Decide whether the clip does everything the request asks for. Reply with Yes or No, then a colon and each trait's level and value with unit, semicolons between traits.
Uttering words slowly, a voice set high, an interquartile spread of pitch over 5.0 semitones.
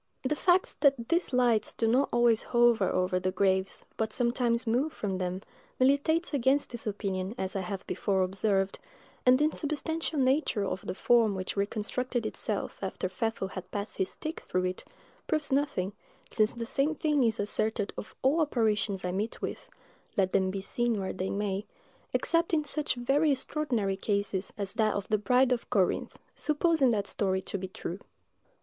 No: average, 175 wpm; high, 220 Hz; wide, 5.5 semitones